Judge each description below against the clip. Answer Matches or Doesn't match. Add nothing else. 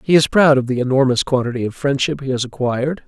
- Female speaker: Doesn't match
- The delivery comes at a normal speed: Doesn't match